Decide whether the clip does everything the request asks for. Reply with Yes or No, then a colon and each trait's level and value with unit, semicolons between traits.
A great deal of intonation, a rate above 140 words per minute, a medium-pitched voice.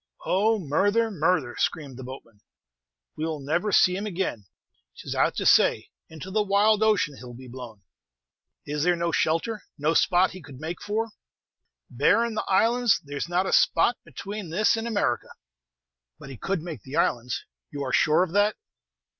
Yes: wide, 6.4 semitones; average, 175 wpm; medium, 175 Hz